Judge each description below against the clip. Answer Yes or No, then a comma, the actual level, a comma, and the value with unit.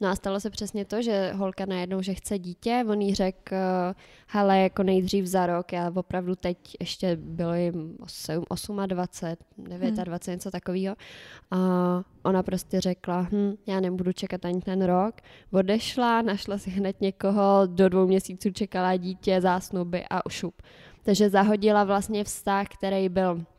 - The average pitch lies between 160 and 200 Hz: Yes, high, 190 Hz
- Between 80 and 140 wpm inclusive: No, average, 165 wpm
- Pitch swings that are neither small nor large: No, narrow, 1.6 semitones